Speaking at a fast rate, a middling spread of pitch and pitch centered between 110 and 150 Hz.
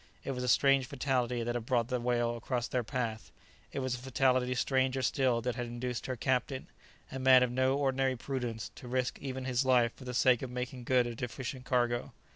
No: fast, 215 wpm; narrow, 1.4 semitones; low, 125 Hz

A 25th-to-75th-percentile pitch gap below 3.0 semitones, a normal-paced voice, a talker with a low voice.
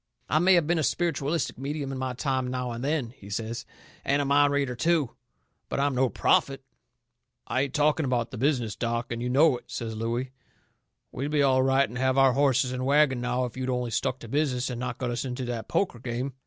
No: narrow, 2.5 semitones; fast, 225 wpm; low, 130 Hz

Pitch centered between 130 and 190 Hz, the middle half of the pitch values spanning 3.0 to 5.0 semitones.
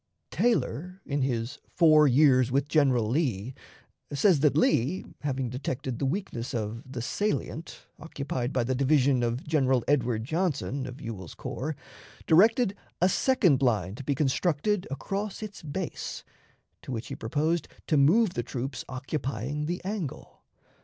Yes: medium, 140 Hz; average, 4.5 semitones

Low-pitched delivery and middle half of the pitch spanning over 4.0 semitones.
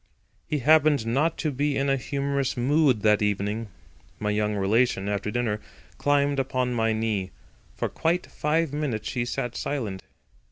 Yes: low, 125 Hz; average, 5.1 semitones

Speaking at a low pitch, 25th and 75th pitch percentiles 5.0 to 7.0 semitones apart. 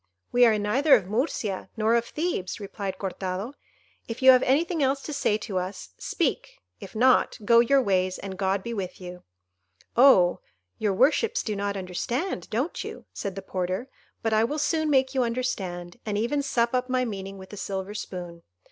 No: high, 215 Hz; average, 5.3 semitones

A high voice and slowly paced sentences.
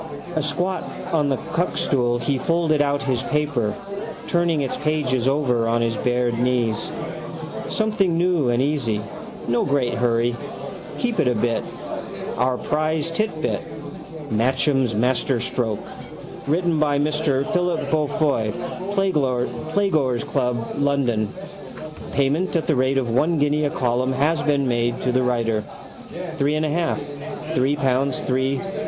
No: medium, 140 Hz; slow, 130 wpm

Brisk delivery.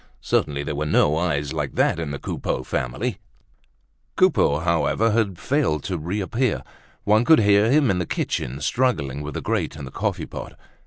No: average, 175 wpm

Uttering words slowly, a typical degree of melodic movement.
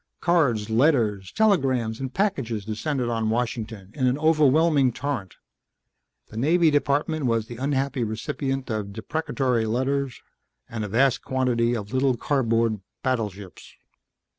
Yes: slow, 125 wpm; average, 4.0 semitones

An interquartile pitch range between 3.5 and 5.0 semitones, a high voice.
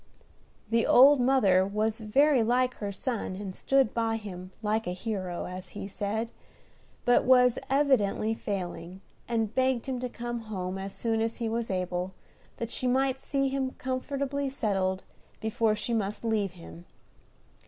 Yes: average, 4.6 semitones; high, 225 Hz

